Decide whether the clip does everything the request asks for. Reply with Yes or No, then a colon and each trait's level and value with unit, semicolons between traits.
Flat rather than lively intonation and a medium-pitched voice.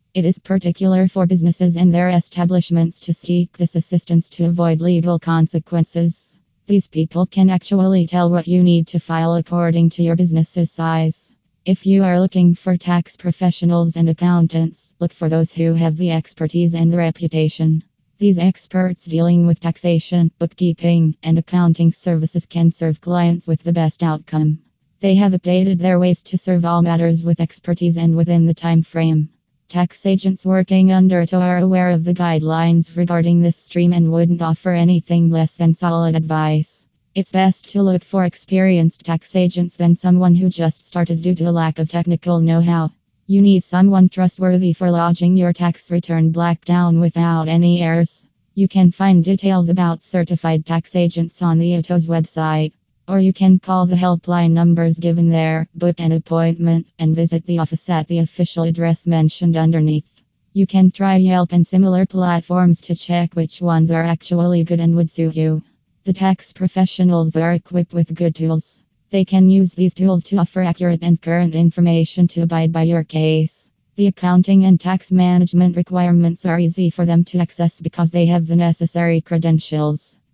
Yes: narrow, 1.5 semitones; medium, 170 Hz